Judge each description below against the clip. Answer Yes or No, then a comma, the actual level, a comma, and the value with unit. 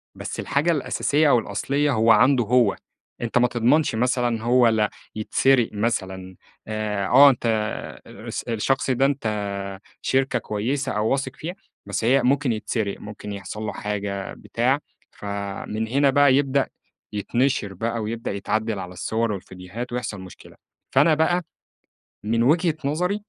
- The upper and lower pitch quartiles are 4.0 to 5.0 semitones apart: Yes, average, 4.4 semitones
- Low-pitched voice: Yes, low, 115 Hz